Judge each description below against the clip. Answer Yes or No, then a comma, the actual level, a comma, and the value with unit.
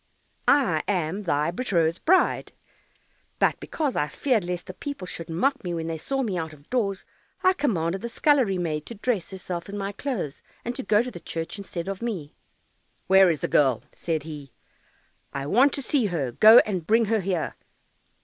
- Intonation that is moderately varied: No, wide, 6.2 semitones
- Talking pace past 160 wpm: Yes, average, 190 wpm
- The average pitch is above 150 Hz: Yes, high, 190 Hz